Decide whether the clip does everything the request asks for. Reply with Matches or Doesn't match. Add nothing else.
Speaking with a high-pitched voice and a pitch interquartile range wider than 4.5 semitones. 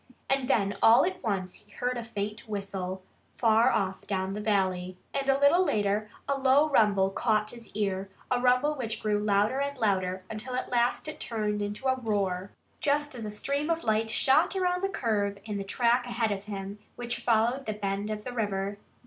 Doesn't match